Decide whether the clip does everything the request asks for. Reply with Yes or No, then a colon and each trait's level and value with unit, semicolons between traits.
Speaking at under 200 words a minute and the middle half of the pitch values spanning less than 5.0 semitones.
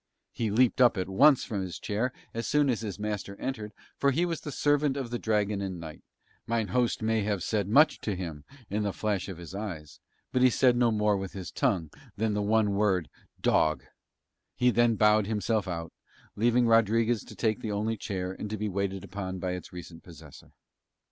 No: fast, 205 wpm; average, 3.5 semitones